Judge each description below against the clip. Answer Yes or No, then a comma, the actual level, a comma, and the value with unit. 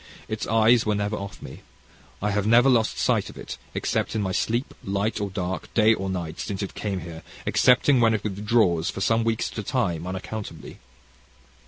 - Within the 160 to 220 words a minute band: Yes, average, 195 wpm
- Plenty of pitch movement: No, average, 3.0 semitones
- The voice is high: No, low, 105 Hz